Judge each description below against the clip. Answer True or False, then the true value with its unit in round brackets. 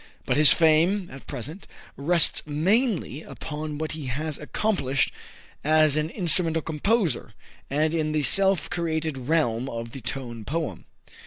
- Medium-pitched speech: True (155 Hz)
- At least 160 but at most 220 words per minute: False (140 wpm)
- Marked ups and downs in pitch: False (3.1 semitones)